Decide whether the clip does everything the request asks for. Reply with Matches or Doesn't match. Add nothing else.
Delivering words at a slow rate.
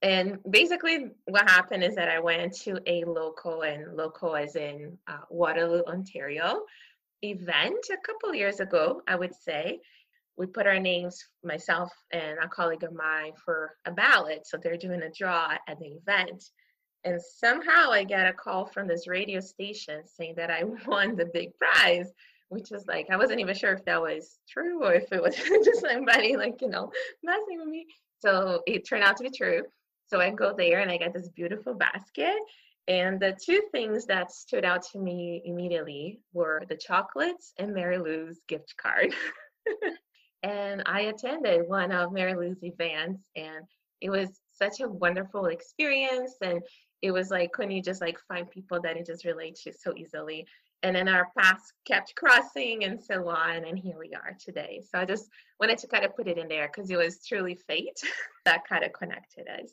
Doesn't match